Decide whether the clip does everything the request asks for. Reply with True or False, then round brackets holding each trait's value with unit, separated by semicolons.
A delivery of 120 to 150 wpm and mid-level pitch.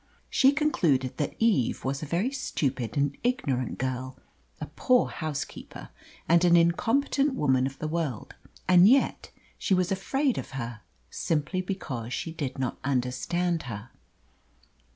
True (140 wpm; 155 Hz)